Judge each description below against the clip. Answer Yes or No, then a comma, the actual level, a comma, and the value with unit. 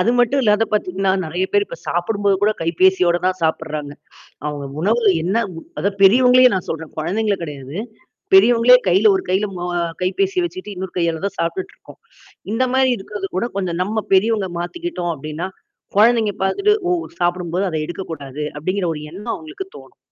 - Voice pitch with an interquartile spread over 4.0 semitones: Yes, average, 4.6 semitones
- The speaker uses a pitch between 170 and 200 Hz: Yes, high, 190 Hz